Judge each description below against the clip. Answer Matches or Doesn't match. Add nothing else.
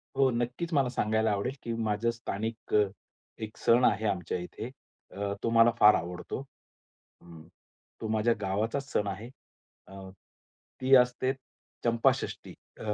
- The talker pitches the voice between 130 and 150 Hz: Doesn't match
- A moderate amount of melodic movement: Matches